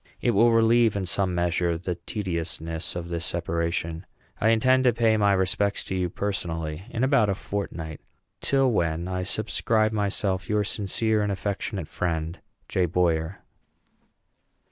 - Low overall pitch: Yes, very low, 95 Hz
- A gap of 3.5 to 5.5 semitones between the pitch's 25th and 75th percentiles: Yes, average, 4.2 semitones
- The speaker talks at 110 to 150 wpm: Yes, average, 145 wpm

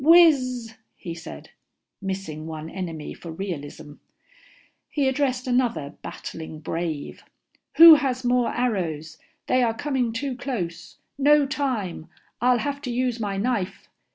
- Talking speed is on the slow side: Yes, slow, 125 wpm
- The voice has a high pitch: Yes, high, 235 Hz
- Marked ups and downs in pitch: Yes, wide, 7.5 semitones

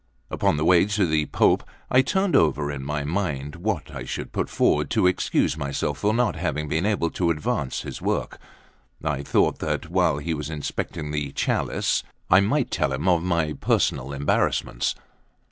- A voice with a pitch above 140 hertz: No, very low, 80 Hz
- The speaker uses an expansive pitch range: No, average, 4.1 semitones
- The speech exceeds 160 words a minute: Yes, average, 180 wpm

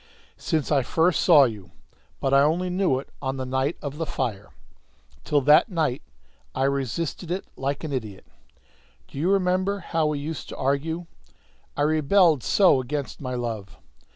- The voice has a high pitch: No, medium, 145 Hz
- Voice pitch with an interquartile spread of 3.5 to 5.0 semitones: Yes, average, 3.9 semitones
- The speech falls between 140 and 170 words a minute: Yes, average, 165 wpm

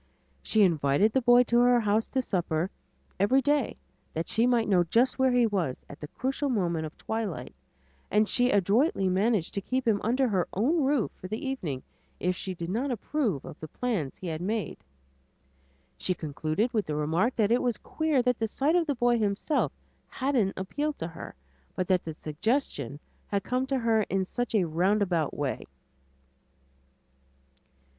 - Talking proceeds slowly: No, average, 180 wpm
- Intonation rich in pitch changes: Yes, wide, 6.0 semitones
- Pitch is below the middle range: No, high, 215 Hz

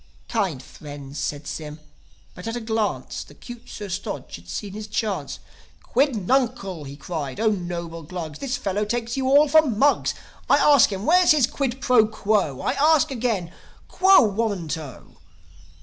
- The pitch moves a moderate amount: No, wide, 7.0 semitones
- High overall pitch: Yes, high, 210 Hz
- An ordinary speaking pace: Yes, average, 165 wpm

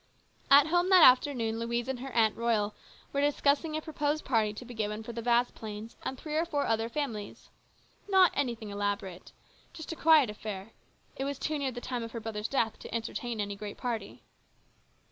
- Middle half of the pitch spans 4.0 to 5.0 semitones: Yes, average, 4.7 semitones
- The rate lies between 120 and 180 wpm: No, average, 190 wpm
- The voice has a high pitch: Yes, high, 235 Hz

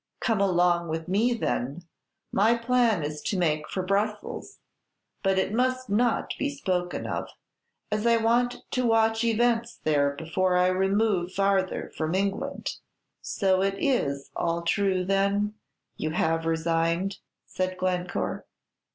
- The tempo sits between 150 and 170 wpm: No, slow, 135 wpm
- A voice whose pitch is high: Yes, high, 195 Hz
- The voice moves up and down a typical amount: Yes, average, 4.3 semitones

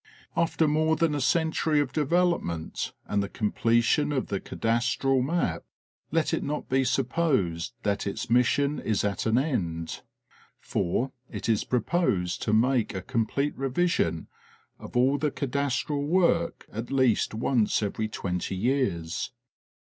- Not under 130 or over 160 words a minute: Yes, average, 140 wpm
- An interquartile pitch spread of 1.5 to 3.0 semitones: No, wide, 5.6 semitones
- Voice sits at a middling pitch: No, low, 130 Hz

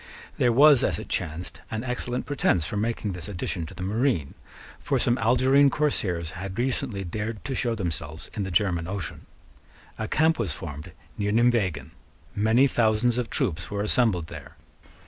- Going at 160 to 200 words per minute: Yes, average, 165 wpm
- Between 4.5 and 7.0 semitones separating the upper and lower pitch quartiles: Yes, wide, 5.6 semitones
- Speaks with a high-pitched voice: No, low, 105 Hz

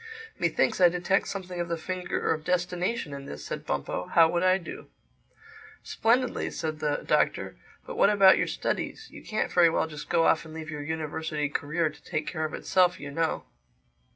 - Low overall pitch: No, medium, 165 Hz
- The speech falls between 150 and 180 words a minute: No, average, 190 wpm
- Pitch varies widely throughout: No, average, 2.9 semitones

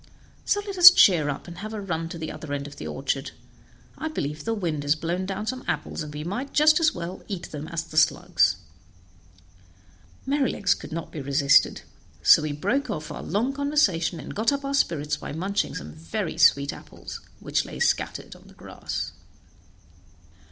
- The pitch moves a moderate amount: No, wide, 7.3 semitones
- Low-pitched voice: No, medium, 170 Hz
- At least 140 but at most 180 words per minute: No, average, 190 wpm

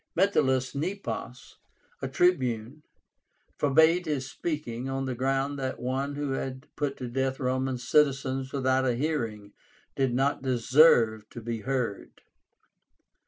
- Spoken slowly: Yes, slow, 125 wpm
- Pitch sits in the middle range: No, low, 130 Hz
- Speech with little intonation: Yes, narrow, 2.2 semitones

